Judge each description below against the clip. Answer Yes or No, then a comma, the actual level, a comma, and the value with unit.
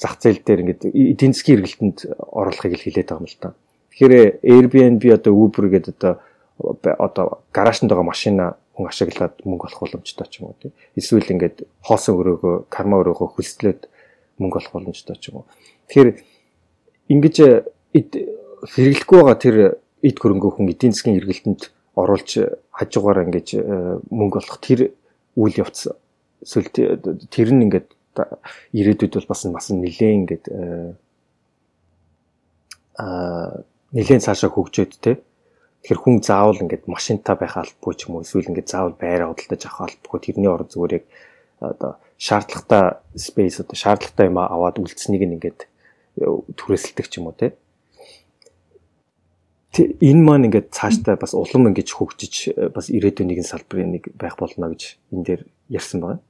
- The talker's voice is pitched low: Yes, low, 100 Hz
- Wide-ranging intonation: Yes, wide, 6.2 semitones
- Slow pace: No, average, 145 wpm